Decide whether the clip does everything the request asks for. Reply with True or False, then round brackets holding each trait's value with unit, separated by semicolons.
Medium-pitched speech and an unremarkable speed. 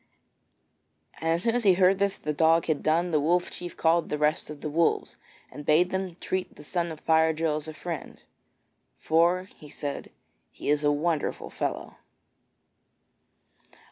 True (165 Hz; 175 wpm)